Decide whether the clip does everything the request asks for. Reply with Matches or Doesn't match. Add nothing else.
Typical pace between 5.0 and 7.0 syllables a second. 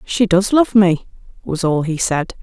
Doesn't match